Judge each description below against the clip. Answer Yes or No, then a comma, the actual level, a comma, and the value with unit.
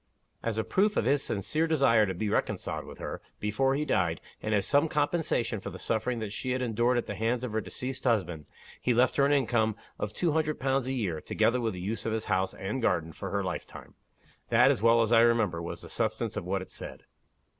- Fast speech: Yes, fast, 235 wpm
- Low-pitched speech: Yes, low, 115 Hz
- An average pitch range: Yes, average, 4.4 semitones